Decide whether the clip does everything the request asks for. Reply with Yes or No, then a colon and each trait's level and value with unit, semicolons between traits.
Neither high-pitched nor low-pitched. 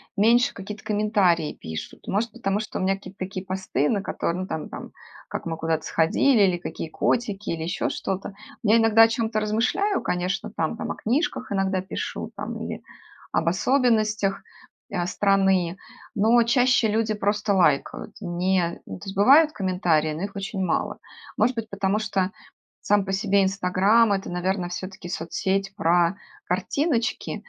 No: high, 195 Hz